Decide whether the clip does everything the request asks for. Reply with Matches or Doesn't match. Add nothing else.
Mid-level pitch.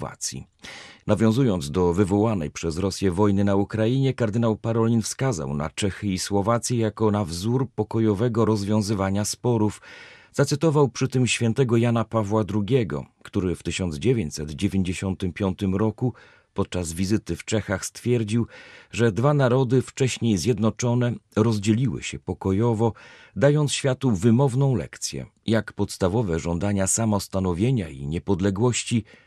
Doesn't match